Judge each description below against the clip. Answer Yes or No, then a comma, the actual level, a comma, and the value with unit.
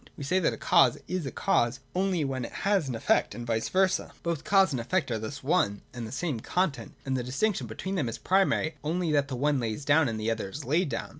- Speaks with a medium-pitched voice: Yes, medium, 145 Hz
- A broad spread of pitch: Yes, wide, 6.9 semitones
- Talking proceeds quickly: Yes, fast, 255 wpm